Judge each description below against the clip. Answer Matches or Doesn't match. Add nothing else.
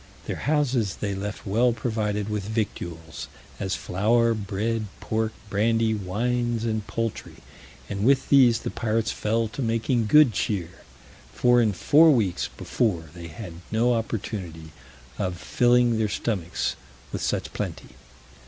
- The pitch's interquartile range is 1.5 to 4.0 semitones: Matches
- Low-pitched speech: Matches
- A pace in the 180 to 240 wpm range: Doesn't match